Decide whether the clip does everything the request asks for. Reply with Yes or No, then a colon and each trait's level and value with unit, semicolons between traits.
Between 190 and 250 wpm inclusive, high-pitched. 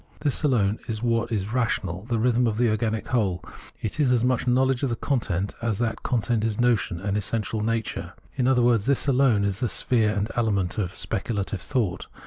No: average, 200 wpm; low, 115 Hz